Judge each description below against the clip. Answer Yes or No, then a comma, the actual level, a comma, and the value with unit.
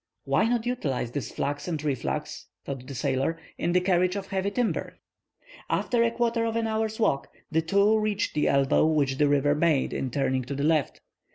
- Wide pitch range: Yes, wide, 7.6 semitones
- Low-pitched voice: No, medium, 160 Hz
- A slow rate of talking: No, average, 195 wpm